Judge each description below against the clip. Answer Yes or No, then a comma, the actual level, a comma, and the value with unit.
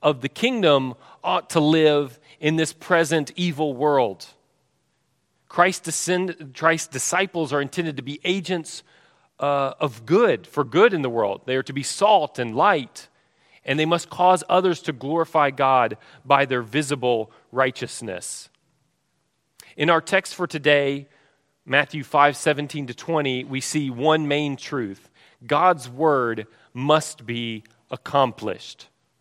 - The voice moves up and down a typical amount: Yes, average, 3.4 semitones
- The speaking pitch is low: No, medium, 150 Hz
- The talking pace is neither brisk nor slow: No, slow, 130 wpm